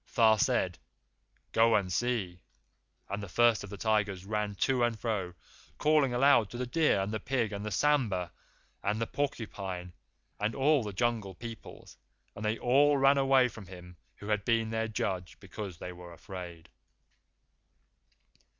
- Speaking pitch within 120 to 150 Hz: No, low, 110 Hz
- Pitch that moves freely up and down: No, average, 3.9 semitones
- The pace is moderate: Yes, average, 160 wpm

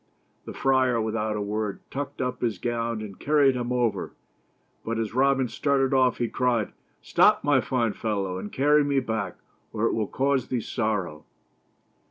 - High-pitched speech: No, low, 120 Hz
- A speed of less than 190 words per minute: Yes, average, 180 wpm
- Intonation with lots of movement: No, average, 3.5 semitones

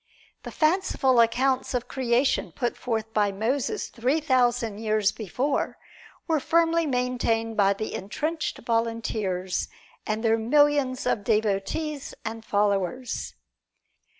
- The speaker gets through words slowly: Yes, slow, 115 wpm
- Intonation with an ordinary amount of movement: Yes, average, 3.6 semitones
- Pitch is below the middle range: No, high, 235 Hz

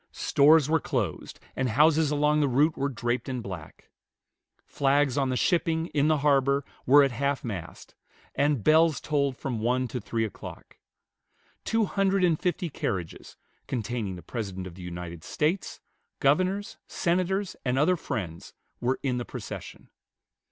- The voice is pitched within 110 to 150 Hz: Yes, medium, 140 Hz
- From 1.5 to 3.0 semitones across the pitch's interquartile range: No, average, 4.6 semitones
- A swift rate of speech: No, average, 150 wpm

